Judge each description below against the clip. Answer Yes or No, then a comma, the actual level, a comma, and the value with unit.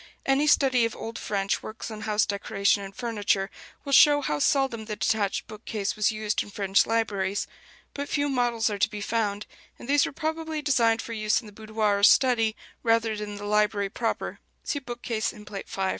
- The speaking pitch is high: Yes, high, 220 Hz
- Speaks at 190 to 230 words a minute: Yes, average, 200 wpm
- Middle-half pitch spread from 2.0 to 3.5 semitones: Yes, average, 2.8 semitones